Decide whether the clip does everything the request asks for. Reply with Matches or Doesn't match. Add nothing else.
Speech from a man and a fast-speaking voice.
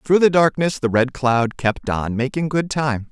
Matches